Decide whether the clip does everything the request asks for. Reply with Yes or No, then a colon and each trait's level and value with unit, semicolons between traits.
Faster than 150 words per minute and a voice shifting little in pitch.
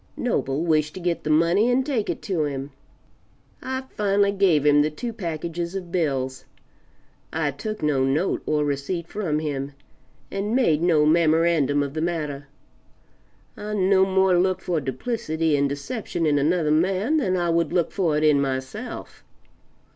No: average, 160 wpm; average, 4.4 semitones